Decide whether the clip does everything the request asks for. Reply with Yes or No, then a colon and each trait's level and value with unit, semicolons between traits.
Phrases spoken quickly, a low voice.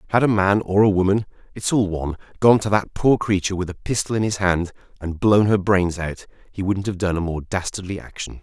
Yes: fast, 220 wpm; very low, 95 Hz